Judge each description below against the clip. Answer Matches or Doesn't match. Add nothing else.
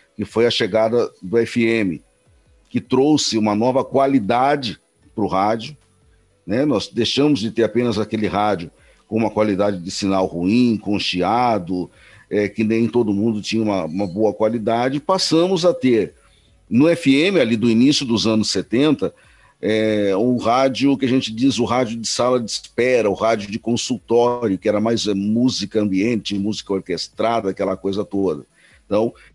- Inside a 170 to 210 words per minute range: Doesn't match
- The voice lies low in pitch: Matches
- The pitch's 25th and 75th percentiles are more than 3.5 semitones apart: Doesn't match